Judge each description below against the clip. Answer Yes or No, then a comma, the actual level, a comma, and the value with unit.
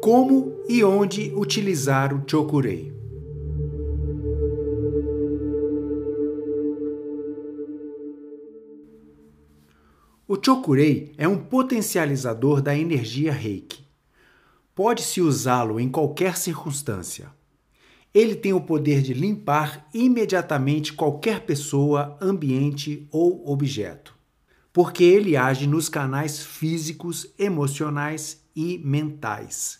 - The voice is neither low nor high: Yes, medium, 150 Hz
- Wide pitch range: No, average, 3.4 semitones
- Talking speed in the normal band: No, slow, 80 wpm